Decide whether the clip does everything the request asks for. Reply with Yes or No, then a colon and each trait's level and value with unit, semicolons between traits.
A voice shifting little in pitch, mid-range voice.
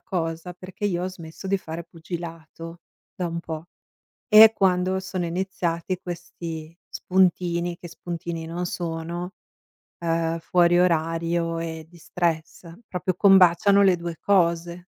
Yes: narrow, 1.6 semitones; medium, 170 Hz